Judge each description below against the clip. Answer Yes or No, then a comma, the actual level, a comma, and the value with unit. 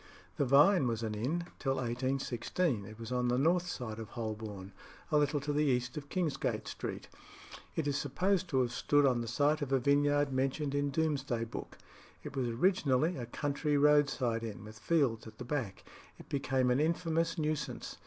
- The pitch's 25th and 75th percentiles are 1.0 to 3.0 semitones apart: No, average, 3.8 semitones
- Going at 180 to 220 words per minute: Yes, average, 185 wpm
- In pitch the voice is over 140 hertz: No, low, 135 Hz